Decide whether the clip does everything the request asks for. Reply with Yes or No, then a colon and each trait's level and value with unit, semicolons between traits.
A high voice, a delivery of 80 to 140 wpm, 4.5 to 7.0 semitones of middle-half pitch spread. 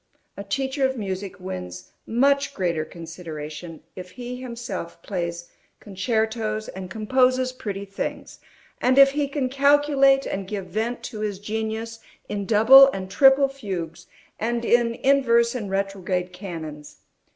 Yes: high, 215 Hz; slow, 135 wpm; wide, 5.5 semitones